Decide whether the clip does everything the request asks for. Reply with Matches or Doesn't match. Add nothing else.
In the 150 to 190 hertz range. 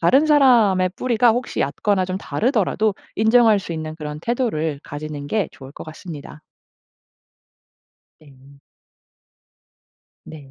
Matches